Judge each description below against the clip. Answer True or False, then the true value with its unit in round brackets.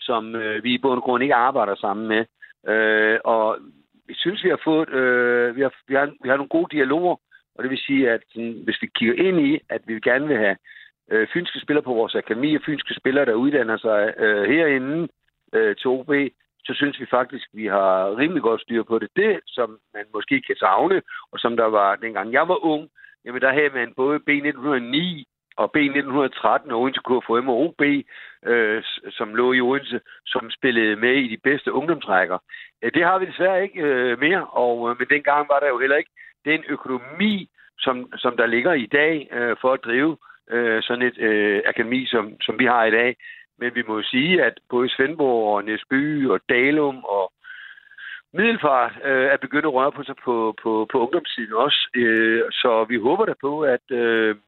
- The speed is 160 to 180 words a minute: False (205 wpm)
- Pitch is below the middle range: True (130 Hz)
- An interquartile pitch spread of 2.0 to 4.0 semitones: False (4.5 semitones)